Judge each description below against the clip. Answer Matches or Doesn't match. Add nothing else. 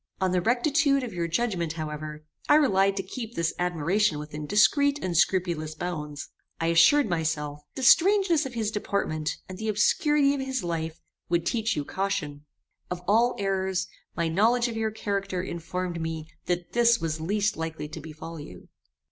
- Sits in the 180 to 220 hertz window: Matches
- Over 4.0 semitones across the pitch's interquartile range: Matches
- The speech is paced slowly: Doesn't match